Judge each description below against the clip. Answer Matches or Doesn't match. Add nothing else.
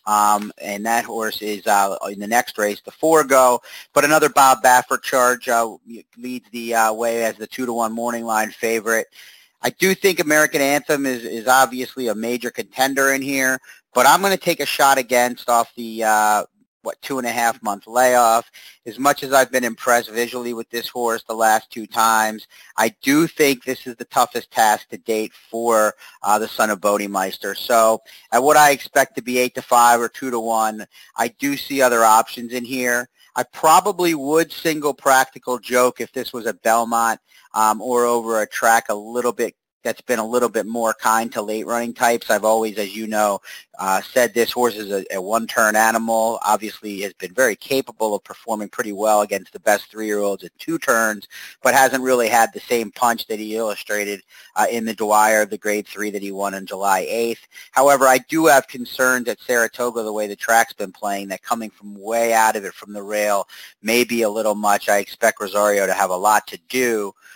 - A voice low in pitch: Matches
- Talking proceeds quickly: Matches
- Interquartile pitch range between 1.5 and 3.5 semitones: Matches